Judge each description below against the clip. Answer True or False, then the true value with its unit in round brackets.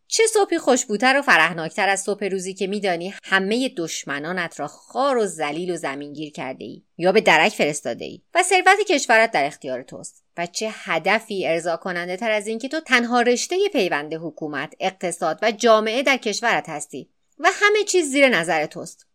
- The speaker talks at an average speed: True (175 wpm)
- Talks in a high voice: True (200 Hz)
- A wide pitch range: True (7.3 semitones)